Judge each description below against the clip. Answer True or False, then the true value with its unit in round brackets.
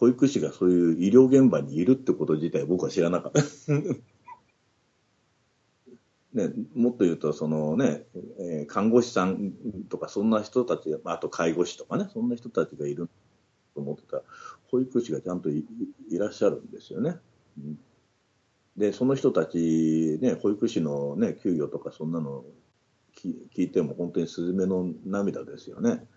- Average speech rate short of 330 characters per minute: True (295 characters per minute)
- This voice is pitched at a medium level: False (110 Hz)